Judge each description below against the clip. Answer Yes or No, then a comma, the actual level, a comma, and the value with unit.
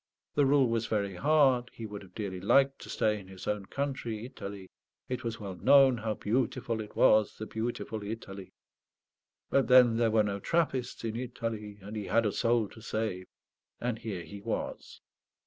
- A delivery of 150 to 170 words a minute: No, average, 180 wpm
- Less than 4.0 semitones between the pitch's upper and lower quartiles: Yes, average, 3.3 semitones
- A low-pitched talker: Yes, low, 110 Hz